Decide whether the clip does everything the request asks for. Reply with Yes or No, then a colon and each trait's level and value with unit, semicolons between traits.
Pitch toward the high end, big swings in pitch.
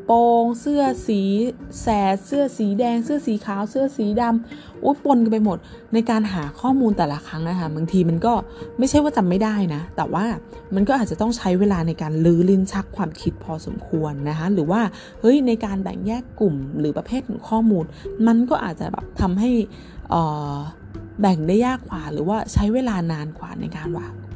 Yes: high, 205 Hz; wide, 5.7 semitones